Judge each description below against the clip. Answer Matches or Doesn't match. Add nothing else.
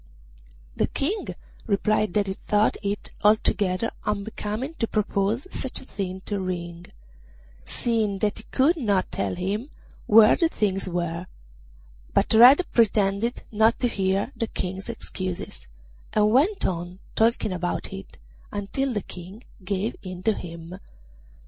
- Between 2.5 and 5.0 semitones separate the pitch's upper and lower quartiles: Matches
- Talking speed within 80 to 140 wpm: Matches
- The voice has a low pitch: Doesn't match